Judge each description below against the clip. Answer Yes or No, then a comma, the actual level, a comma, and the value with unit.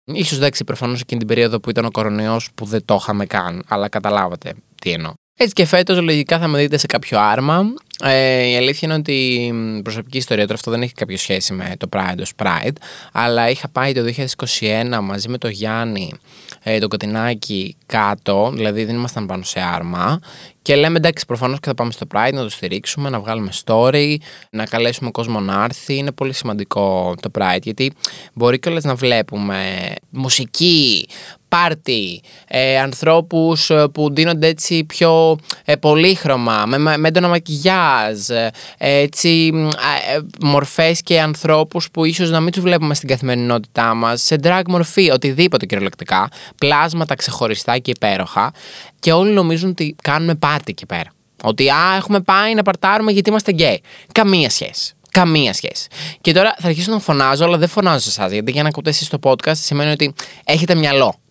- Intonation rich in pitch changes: Yes, wide, 6.4 semitones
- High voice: No, low, 135 Hz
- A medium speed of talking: No, fast, 175 wpm